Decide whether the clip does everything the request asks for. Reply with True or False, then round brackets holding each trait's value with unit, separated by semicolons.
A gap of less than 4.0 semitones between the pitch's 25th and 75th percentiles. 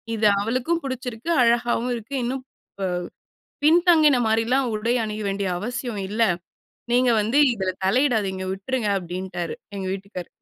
False (4.3 semitones)